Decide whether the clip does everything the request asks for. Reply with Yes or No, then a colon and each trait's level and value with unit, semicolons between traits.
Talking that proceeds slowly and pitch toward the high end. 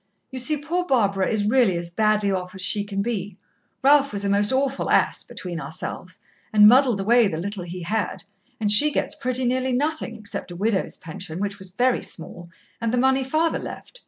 No: average, 200 wpm; high, 215 Hz